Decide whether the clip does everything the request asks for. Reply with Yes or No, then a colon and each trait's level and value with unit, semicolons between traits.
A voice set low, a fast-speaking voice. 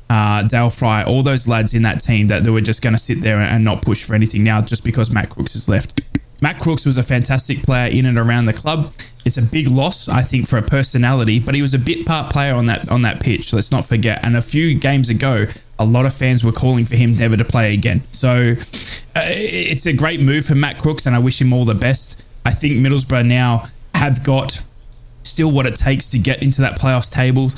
Yes: low, 125 Hz; fast, 245 wpm